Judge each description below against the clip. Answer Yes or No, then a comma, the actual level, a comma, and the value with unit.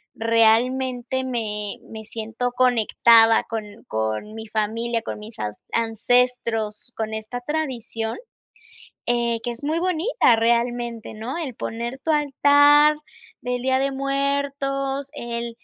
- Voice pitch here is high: Yes, high, 240 Hz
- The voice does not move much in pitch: No, average, 3.3 semitones